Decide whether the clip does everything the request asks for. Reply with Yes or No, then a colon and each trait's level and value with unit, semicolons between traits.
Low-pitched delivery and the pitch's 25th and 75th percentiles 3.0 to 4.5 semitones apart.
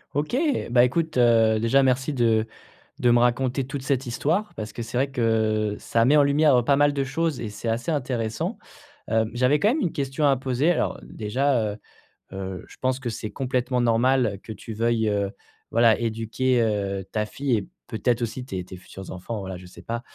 Yes: low, 120 Hz; average, 3.5 semitones